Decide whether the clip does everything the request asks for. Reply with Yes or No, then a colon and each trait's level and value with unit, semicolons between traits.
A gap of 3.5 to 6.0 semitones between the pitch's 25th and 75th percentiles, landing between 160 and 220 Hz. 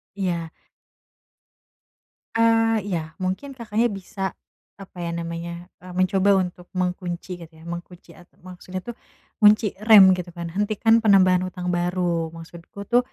No: average, 2.9 semitones; medium, 185 Hz